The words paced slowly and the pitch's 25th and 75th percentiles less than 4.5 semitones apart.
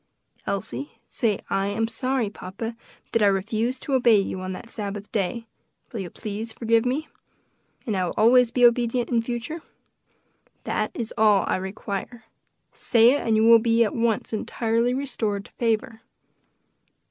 No: average, 165 wpm; narrow, 2.6 semitones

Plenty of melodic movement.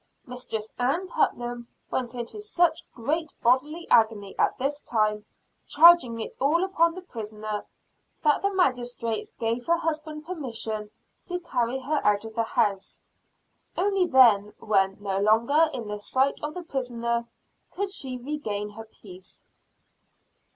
Yes: wide, 6.2 semitones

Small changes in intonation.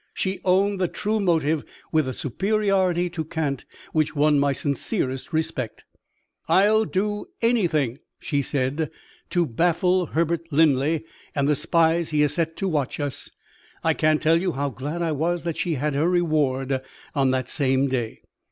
No: average, 3.8 semitones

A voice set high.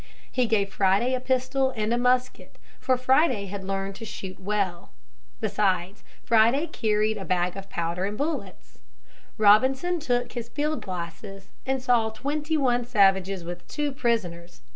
Yes: high, 220 Hz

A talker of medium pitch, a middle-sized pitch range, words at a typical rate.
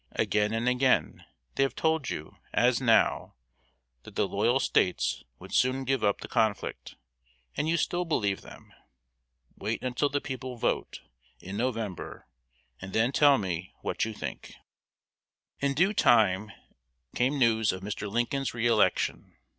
No: low, 120 Hz; average, 4.4 semitones; average, 145 wpm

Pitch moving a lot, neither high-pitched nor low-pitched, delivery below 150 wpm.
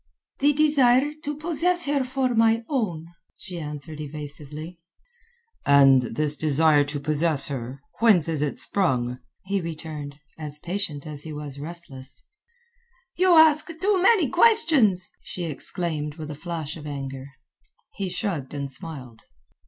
Yes: wide, 8.2 semitones; medium, 160 Hz; slow, 135 wpm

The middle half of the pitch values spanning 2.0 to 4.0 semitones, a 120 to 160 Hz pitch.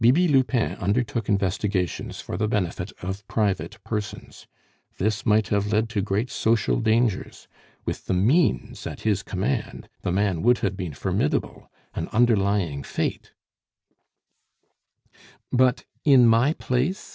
No: average, 3.7 semitones; low, 105 Hz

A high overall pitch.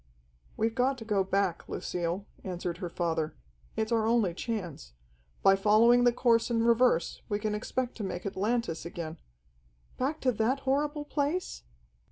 Yes: high, 215 Hz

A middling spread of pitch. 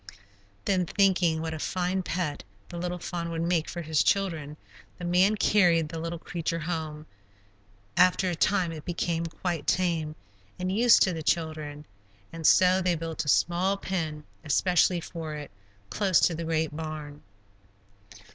No: narrow, 2.3 semitones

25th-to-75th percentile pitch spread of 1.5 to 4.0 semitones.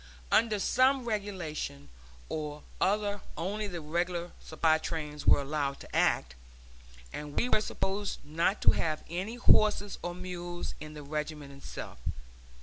No: average, 5.1 semitones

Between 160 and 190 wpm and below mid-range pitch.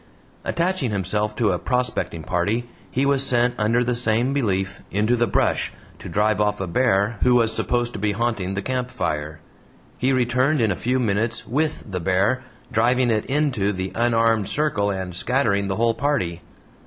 Yes: average, 175 wpm; low, 115 Hz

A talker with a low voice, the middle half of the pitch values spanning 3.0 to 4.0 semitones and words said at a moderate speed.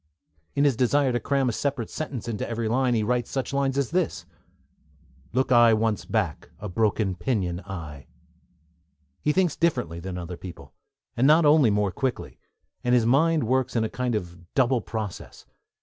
No: low, 120 Hz; average, 4.7 semitones; average, 170 wpm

